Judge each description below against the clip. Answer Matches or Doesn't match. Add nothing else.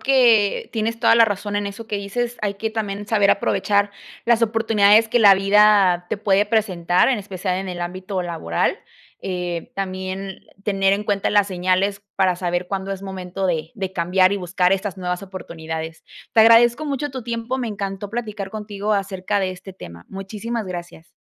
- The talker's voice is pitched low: Doesn't match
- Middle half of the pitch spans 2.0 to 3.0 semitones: Matches